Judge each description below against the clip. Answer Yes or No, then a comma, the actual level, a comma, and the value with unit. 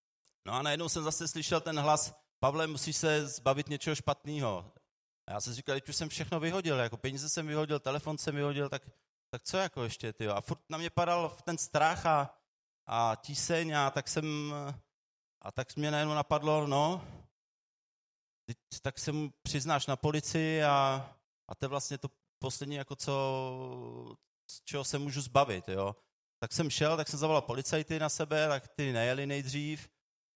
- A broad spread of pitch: No, narrow, 2.5 semitones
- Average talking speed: No, fast, 175 wpm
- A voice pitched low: No, medium, 145 Hz